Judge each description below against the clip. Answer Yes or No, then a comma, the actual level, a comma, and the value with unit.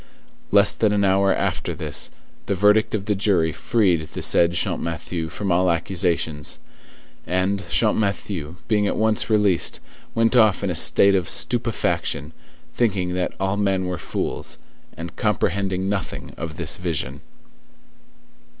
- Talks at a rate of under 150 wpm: Yes, average, 140 wpm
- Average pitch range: Yes, average, 3.2 semitones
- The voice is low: Yes, very low, 95 Hz